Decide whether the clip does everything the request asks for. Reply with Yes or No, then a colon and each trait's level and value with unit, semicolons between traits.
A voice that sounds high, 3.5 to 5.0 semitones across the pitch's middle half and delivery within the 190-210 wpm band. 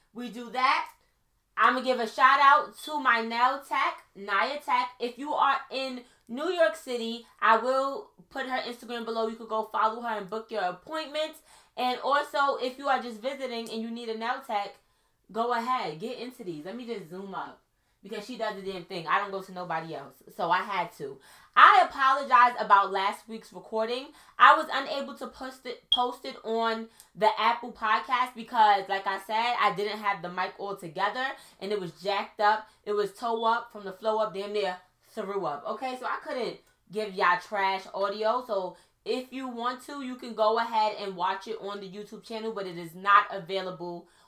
Yes: high, 225 Hz; average, 4.1 semitones; fast, 205 wpm